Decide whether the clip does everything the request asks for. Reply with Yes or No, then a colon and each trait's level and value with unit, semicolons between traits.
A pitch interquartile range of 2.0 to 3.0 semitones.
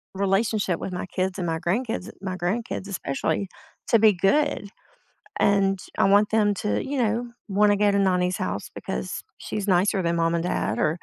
Yes: narrow, 2.6 semitones